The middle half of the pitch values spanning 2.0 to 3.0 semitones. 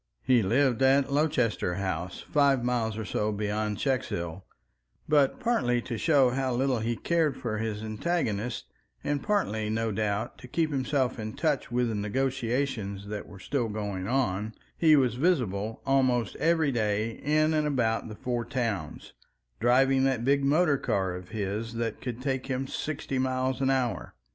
No: average, 4.1 semitones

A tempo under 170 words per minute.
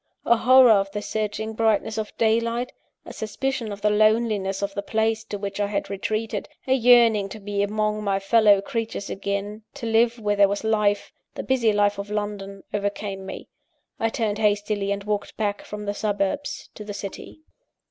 No: average, 185 wpm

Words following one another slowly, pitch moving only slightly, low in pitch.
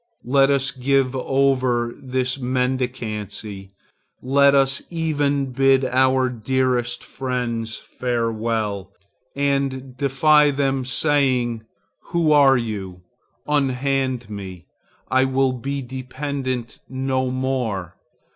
Yes: slow, 95 wpm; narrow, 2.1 semitones; low, 130 Hz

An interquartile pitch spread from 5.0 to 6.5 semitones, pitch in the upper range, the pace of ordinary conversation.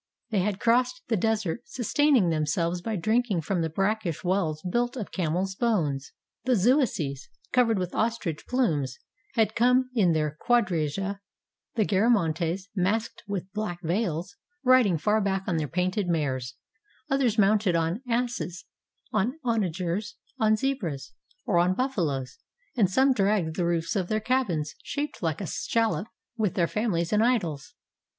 Yes: wide, 5.4 semitones; high, 195 Hz; average, 150 wpm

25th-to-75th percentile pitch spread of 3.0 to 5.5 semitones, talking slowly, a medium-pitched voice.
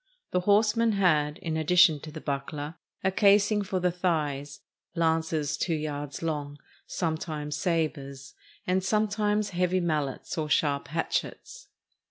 Yes: average, 4.1 semitones; slow, 130 wpm; medium, 160 Hz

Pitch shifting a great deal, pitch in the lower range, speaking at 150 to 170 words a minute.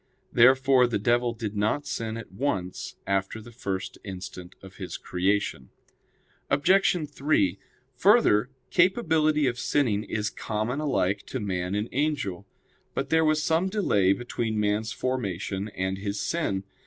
No: wide, 6.5 semitones; low, 110 Hz; average, 140 wpm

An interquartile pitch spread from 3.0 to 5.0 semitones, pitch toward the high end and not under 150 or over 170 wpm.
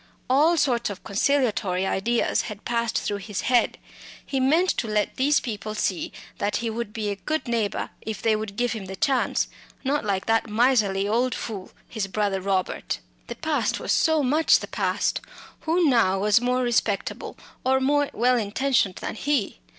Yes: average, 4.5 semitones; high, 230 Hz; average, 165 wpm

